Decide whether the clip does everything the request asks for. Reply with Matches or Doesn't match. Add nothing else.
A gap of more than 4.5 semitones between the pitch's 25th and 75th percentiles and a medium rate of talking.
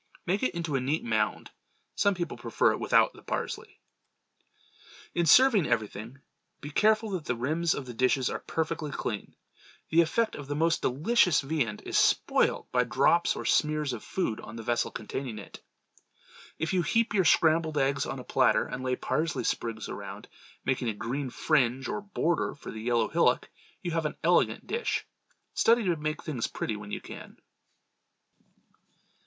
Matches